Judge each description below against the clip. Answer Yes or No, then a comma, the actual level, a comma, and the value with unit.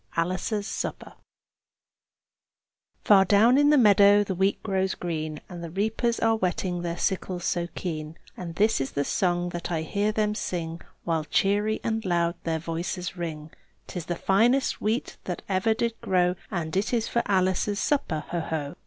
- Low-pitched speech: No, medium, 185 Hz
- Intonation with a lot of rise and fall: No, average, 3.6 semitones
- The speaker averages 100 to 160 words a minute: No, average, 170 wpm